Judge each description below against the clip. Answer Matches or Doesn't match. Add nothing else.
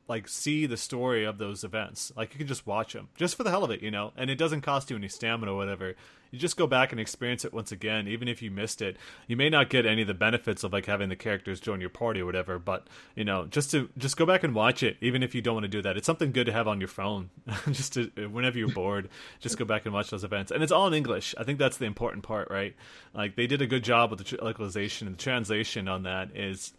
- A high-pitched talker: Doesn't match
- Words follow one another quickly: Matches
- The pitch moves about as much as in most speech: Matches